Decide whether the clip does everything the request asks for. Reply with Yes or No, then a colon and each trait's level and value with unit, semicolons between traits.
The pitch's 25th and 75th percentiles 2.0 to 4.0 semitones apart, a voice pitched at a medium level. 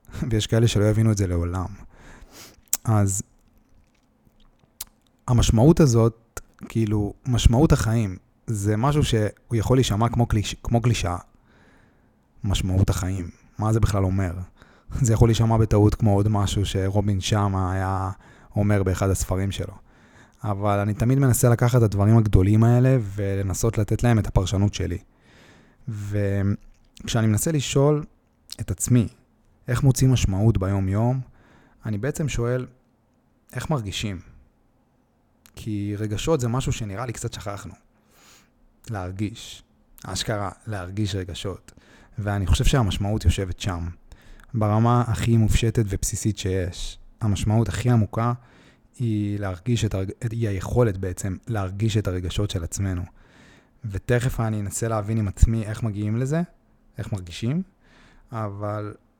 No: average, 3.1 semitones; low, 110 Hz